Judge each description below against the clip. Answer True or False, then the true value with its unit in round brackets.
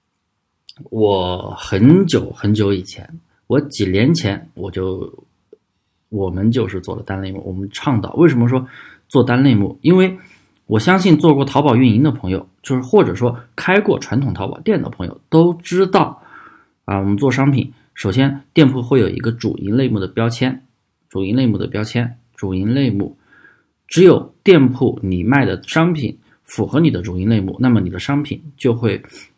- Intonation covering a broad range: True (5.8 semitones)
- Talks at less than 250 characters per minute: False (255 characters per minute)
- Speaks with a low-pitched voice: True (120 Hz)